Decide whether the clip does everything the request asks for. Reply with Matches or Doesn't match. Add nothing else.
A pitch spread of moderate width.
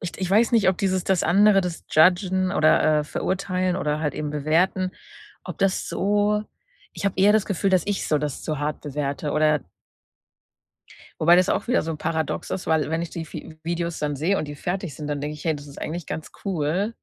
Matches